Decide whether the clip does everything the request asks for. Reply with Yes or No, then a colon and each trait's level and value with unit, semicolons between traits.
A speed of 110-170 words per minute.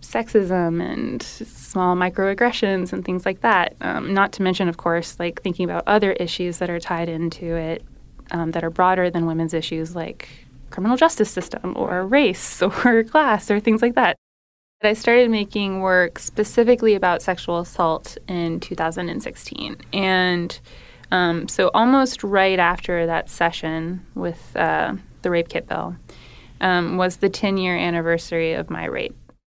Yes: average, 155 wpm